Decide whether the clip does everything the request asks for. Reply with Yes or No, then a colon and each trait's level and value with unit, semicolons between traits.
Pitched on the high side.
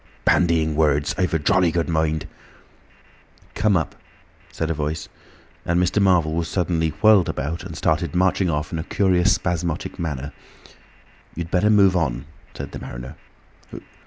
No: very low, 85 Hz